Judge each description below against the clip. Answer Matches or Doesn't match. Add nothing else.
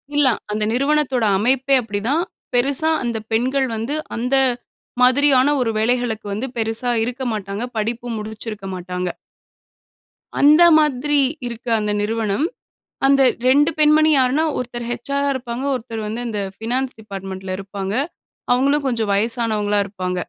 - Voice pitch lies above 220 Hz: Matches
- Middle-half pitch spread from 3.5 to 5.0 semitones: Matches